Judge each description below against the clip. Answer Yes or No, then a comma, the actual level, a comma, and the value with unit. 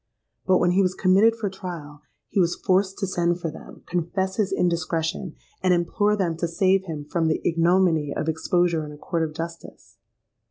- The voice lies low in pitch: No, medium, 175 Hz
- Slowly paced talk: No, average, 190 wpm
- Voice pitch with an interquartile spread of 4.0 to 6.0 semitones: No, narrow, 2.5 semitones